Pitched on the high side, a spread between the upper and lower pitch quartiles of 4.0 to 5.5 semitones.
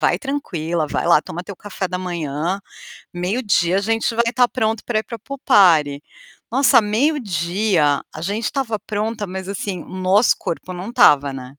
Yes: high, 195 Hz; average, 4.7 semitones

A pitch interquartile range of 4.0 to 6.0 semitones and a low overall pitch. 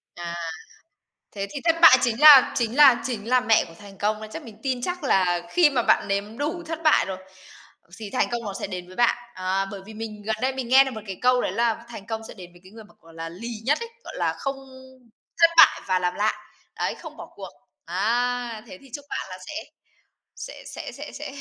No: average, 5.0 semitones; high, 225 Hz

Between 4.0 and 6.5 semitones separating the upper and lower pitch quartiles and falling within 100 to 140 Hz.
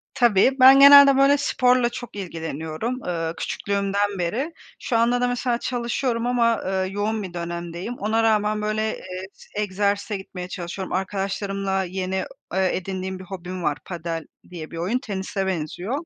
No: average, 4.3 semitones; high, 195 Hz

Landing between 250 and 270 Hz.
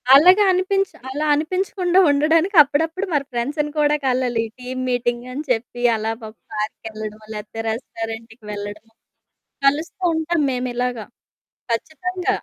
Yes: very high, 260 Hz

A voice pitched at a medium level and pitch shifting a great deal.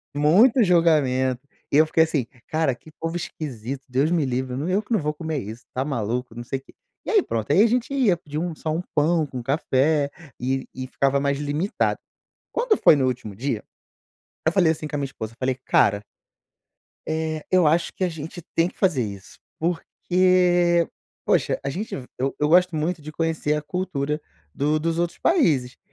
No: medium, 150 Hz; average, 4.5 semitones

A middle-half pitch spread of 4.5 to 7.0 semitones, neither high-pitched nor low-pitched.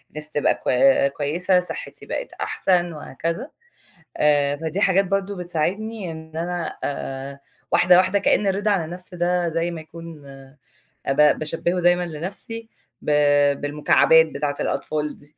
No: average, 3.4 semitones; medium, 165 Hz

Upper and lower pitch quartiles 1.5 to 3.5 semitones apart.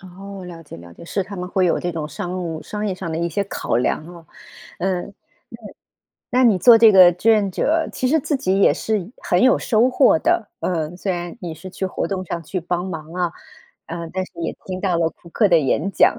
Yes: average, 2.9 semitones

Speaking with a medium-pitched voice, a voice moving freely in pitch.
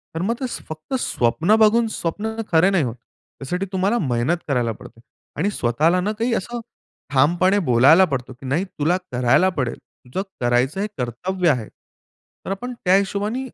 Yes: medium, 175 Hz; wide, 7.5 semitones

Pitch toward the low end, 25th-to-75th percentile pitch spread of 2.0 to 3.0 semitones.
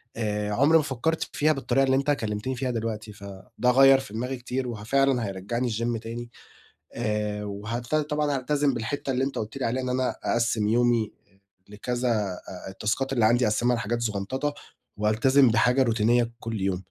No: low, 120 Hz; average, 3.7 semitones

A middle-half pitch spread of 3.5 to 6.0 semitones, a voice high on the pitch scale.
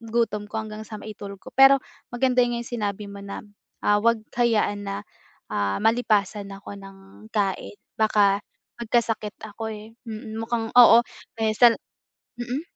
No: narrow, 2.4 semitones; high, 215 Hz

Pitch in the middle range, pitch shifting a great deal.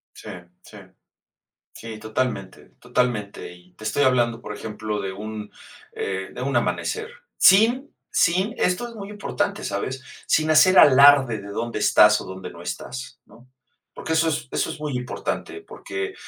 No: low, 125 Hz; wide, 7.7 semitones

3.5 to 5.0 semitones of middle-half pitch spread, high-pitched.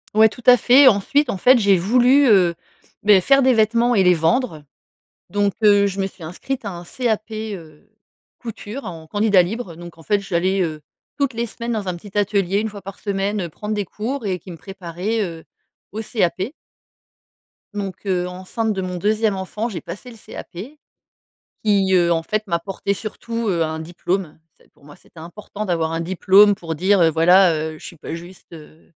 Yes: average, 4.0 semitones; high, 195 Hz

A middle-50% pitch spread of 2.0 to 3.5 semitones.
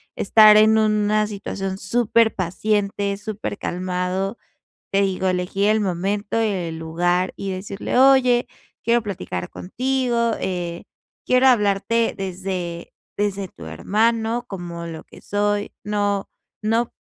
Yes: average, 2.9 semitones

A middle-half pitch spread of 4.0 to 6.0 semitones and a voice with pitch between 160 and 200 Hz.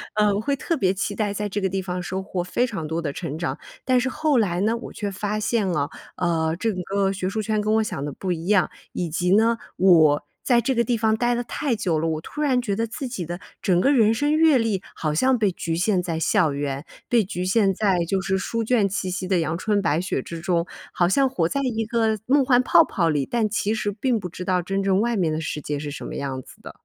Yes: average, 4.6 semitones; high, 195 Hz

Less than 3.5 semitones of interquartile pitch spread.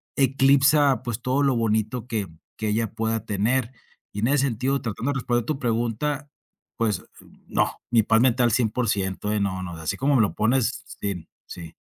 No: average, 3.8 semitones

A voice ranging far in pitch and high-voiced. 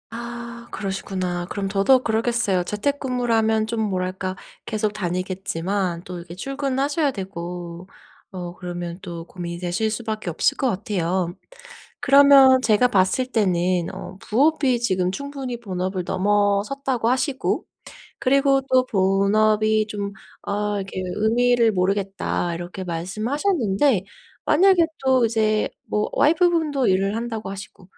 No: average, 4.8 semitones; high, 210 Hz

